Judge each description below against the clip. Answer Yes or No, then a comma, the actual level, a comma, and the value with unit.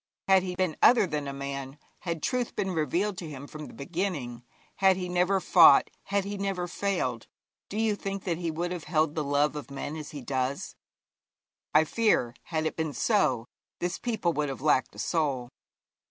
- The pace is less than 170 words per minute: No, average, 195 wpm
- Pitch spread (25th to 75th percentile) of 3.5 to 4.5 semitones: No, average, 4.9 semitones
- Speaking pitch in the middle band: Yes, medium, 160 Hz